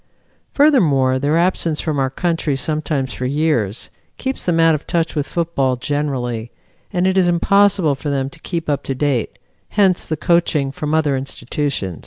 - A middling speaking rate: Yes, average, 170 wpm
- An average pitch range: Yes, average, 3.9 semitones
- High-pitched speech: No, medium, 150 Hz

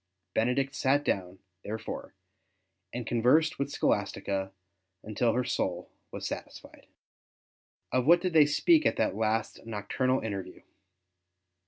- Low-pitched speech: Yes, low, 125 Hz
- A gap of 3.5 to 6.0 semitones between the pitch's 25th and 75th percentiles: Yes, average, 4.9 semitones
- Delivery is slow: Yes, slow, 120 wpm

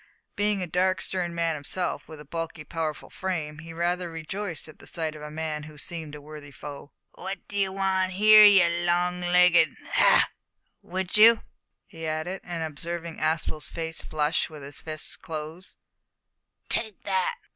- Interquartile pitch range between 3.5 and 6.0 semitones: No, average, 3.0 semitones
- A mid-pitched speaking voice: Yes, medium, 170 Hz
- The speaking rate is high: No, average, 165 wpm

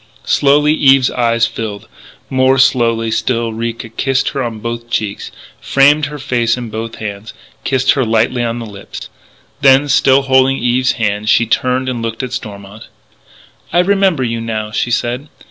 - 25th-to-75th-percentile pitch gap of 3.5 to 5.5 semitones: No, average, 2.8 semitones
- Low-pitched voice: Yes, low, 120 Hz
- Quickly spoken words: No, average, 165 wpm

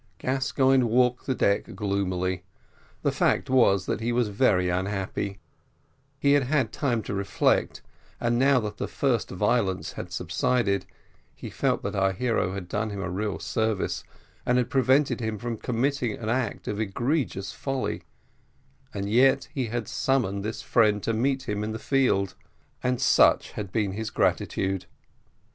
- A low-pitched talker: Yes, low, 110 Hz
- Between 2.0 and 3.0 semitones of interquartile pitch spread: No, average, 4.3 semitones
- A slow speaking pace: No, average, 160 wpm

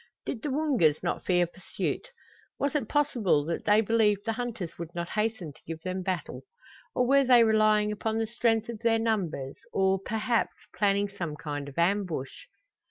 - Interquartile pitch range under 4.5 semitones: No, average, 4.8 semitones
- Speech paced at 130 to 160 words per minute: No, average, 175 wpm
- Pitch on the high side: Yes, high, 210 Hz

